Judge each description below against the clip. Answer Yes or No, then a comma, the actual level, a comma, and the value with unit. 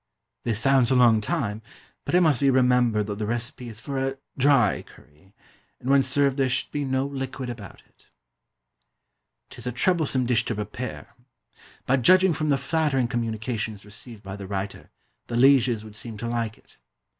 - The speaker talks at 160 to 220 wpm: Yes, average, 180 wpm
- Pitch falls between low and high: No, low, 125 Hz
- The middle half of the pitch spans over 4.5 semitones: No, average, 3.7 semitones